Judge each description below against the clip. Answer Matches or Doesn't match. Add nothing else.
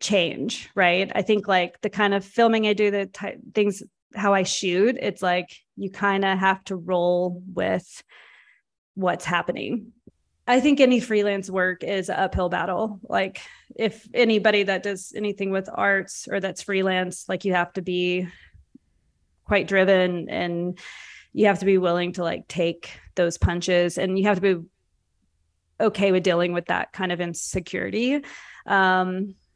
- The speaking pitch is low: Doesn't match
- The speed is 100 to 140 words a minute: Doesn't match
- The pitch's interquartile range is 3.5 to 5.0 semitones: Doesn't match